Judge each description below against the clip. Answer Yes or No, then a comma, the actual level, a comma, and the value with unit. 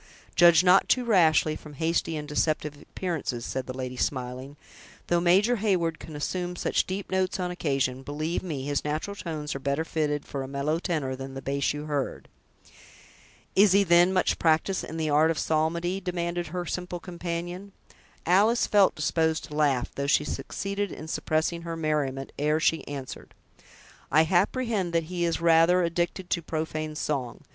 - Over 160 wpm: Yes, average, 170 wpm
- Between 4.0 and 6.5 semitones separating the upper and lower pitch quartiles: No, average, 3.2 semitones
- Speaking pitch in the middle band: Yes, medium, 160 Hz